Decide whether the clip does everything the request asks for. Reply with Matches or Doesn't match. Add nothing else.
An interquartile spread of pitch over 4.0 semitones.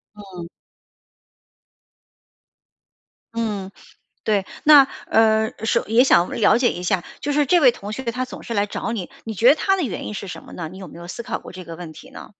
Matches